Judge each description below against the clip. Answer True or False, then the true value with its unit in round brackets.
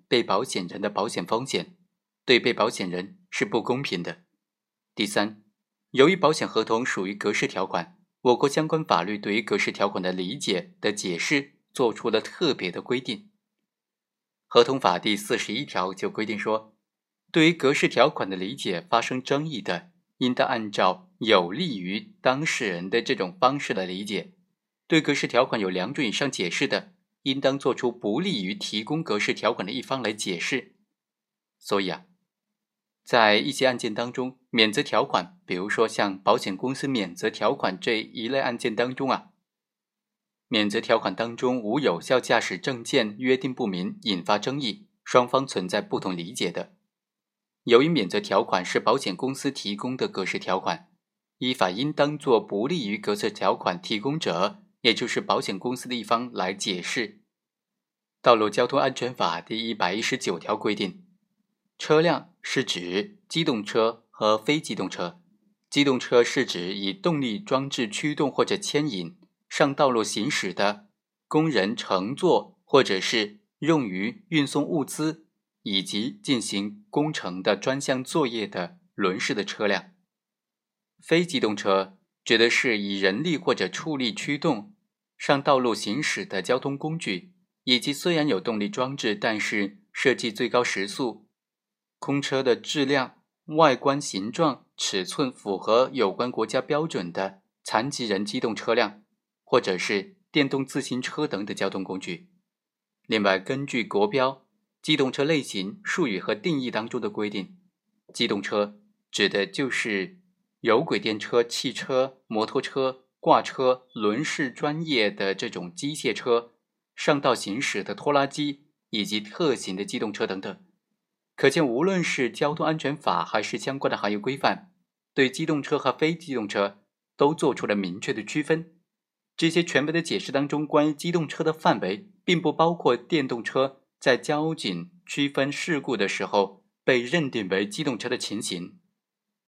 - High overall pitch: False (135 Hz)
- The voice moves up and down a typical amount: False (7.4 semitones)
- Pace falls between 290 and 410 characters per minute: False (240 characters per minute)